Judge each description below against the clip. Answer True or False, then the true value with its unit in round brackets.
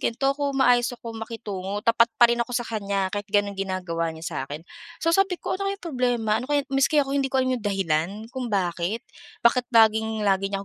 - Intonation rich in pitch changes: False (4.8 semitones)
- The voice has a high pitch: True (225 Hz)